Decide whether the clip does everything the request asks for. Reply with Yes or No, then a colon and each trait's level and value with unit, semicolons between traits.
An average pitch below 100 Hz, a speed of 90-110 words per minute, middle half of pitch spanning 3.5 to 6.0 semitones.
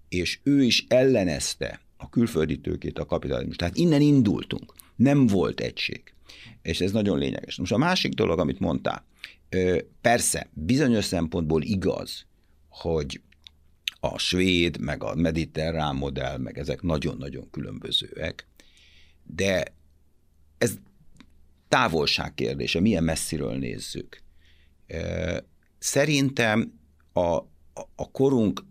Yes: very low, 80 Hz; slow, 105 wpm; average, 3.9 semitones